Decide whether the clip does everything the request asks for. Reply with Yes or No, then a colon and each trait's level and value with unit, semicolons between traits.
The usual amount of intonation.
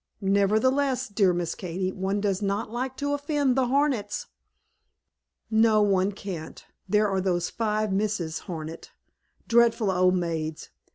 Yes: average, 4.2 semitones